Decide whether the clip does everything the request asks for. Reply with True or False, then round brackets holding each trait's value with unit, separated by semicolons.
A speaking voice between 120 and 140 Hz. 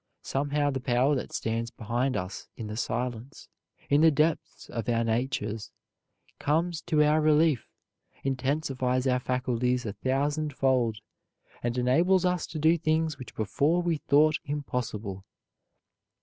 True (135 Hz)